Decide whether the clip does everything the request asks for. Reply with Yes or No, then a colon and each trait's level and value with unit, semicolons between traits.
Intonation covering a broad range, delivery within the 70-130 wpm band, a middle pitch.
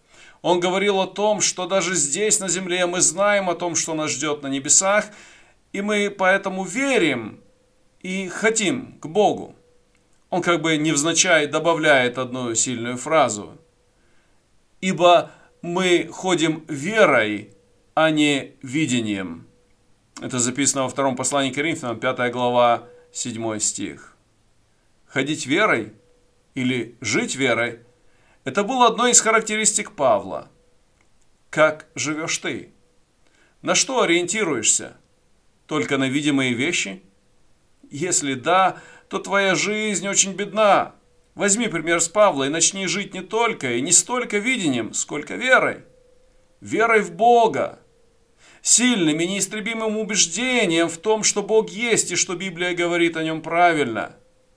Yes: wide, 6.7 semitones; average, 125 wpm; medium, 170 Hz